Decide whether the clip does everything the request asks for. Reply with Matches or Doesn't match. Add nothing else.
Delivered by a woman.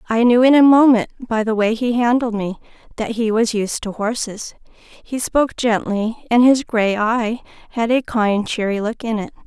Matches